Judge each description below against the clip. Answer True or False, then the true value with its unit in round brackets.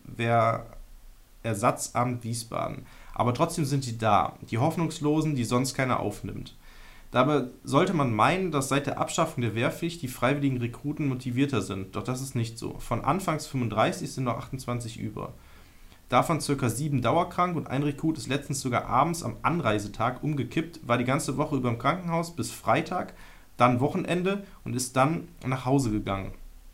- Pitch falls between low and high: False (130 Hz)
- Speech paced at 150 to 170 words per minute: True (160 wpm)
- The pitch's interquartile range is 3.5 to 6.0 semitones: True (4.2 semitones)